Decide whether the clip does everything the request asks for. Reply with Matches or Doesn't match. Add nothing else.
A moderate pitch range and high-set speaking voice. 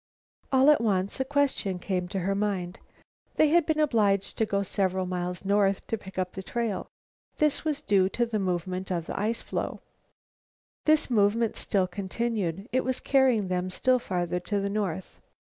Matches